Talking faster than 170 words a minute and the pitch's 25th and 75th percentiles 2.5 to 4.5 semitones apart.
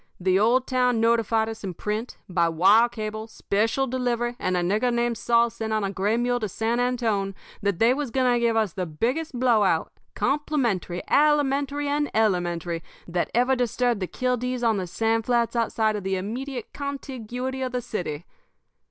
Yes: average, 180 wpm; average, 3.7 semitones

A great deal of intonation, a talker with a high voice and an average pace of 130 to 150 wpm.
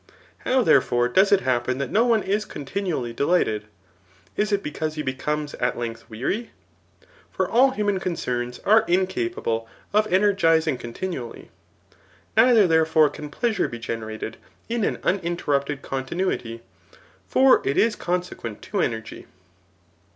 No: wide, 8.5 semitones; medium, 160 Hz; slow, 135 wpm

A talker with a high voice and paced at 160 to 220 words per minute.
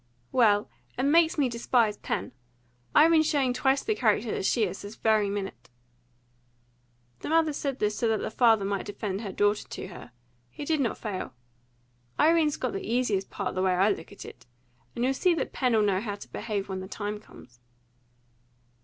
Yes: high, 220 Hz; average, 190 wpm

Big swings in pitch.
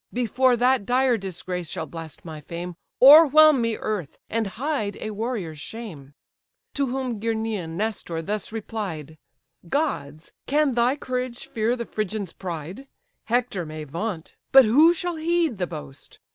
Yes: wide, 6.9 semitones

